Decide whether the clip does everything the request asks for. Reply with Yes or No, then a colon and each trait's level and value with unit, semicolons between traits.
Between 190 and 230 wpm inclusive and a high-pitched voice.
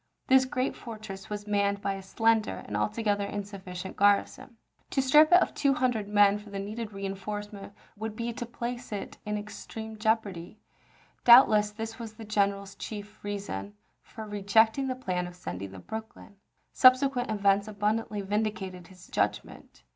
No: average, 155 wpm; high, 210 Hz